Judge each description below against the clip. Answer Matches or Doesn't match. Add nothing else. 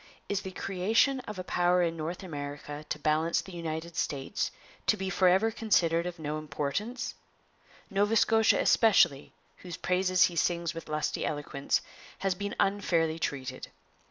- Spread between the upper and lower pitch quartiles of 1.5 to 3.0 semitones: Doesn't match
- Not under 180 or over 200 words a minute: Doesn't match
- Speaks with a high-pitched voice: Doesn't match